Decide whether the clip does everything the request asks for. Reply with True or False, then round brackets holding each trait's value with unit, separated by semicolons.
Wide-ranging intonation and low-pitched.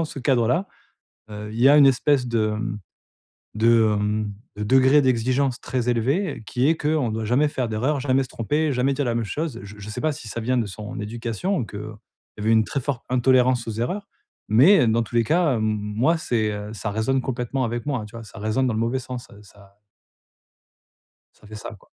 False (3.7 semitones; 120 Hz)